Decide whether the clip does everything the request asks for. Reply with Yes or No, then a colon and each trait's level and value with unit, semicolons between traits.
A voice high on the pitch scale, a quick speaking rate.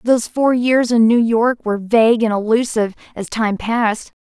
No: high, 230 Hz; average, 185 wpm